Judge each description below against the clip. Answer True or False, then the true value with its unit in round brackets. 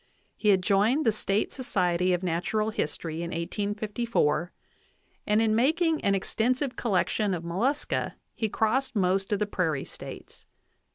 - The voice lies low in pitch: False (205 Hz)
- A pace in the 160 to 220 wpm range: False (145 wpm)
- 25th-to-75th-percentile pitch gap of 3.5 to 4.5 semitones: True (4.1 semitones)